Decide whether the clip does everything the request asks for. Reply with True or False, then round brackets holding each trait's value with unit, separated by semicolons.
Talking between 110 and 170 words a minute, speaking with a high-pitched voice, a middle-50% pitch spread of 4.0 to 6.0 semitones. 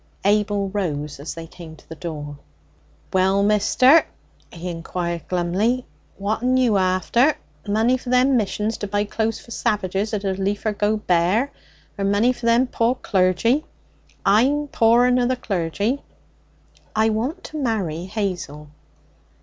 True (140 wpm; 205 Hz; 4.5 semitones)